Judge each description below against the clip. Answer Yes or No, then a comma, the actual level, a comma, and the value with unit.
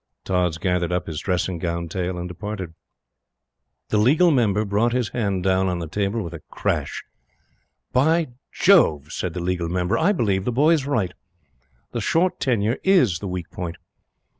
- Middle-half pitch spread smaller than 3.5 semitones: No, wide, 5.4 semitones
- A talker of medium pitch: No, very low, 95 Hz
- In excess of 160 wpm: Yes, average, 170 wpm